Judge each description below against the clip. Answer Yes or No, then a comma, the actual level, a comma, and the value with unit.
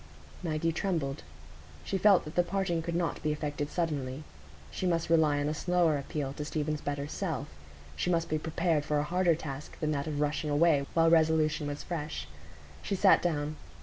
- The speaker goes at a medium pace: Yes, average, 185 wpm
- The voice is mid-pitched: Yes, medium, 155 Hz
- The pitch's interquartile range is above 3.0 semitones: No, narrow, 2.5 semitones